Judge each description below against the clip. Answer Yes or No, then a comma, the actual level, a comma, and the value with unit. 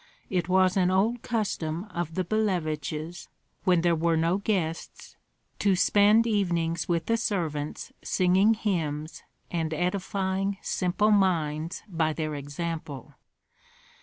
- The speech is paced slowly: Yes, slow, 120 wpm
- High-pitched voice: No, medium, 175 Hz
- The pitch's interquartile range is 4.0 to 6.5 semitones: No, average, 3.5 semitones